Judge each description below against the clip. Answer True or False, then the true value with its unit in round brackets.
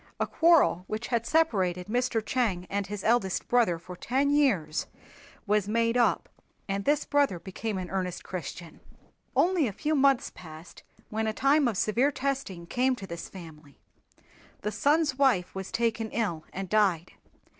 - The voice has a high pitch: True (215 Hz)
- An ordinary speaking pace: True (160 wpm)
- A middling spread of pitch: False (6.1 semitones)